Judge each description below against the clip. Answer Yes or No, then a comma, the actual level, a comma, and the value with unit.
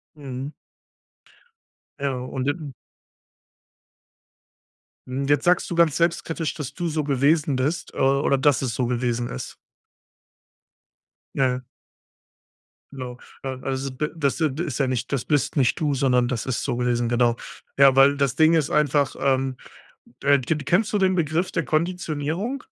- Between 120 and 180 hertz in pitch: Yes, medium, 140 Hz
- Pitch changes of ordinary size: Yes, average, 3.3 semitones